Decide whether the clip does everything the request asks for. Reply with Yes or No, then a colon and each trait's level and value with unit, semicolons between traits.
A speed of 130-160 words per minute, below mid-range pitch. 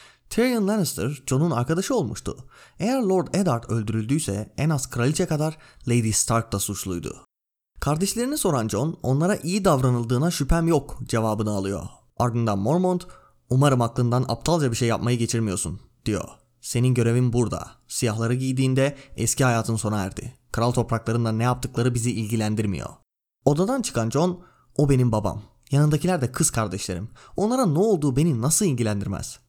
Yes: fast, 140 wpm; low, 125 Hz